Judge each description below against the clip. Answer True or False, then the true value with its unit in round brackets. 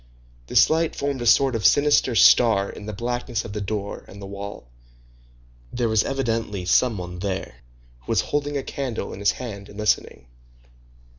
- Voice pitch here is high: False (110 Hz)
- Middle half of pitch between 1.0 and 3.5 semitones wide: False (4.2 semitones)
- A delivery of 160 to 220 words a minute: True (175 wpm)